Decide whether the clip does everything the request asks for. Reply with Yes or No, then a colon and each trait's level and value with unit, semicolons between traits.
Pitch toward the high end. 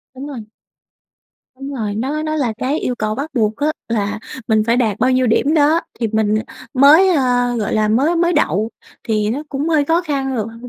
Yes: very high, 255 Hz